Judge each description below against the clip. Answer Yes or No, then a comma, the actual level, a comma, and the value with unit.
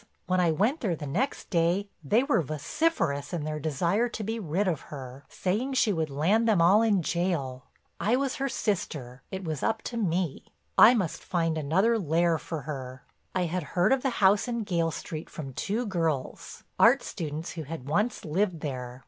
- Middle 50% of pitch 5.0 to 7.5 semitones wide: Yes, wide, 5.6 semitones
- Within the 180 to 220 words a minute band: Yes, average, 190 wpm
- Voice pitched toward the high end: No, medium, 175 Hz